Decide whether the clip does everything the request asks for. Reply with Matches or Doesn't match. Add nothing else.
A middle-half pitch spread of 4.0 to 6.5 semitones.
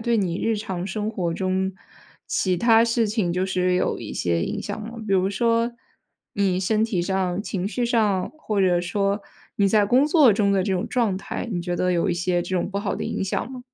Doesn't match